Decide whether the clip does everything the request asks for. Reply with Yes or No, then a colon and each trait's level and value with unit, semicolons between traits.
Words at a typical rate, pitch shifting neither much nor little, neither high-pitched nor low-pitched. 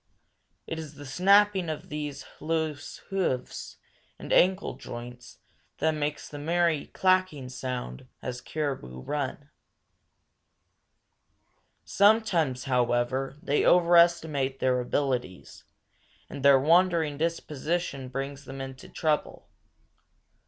No: slow, 100 wpm; average, 4.2 semitones; medium, 145 Hz